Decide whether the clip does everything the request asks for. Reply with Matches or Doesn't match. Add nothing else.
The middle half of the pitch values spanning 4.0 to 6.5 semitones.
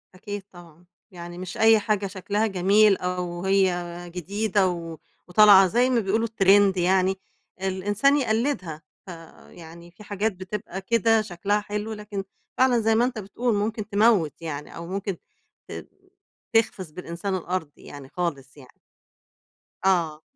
Doesn't match